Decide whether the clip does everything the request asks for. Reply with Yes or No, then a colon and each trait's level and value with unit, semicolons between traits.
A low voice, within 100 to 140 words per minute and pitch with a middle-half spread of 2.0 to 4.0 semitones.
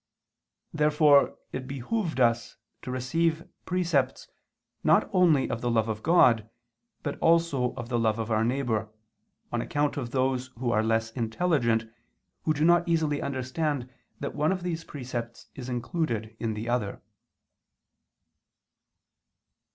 No: low, 130 Hz; slow, 135 wpm; average, 5.0 semitones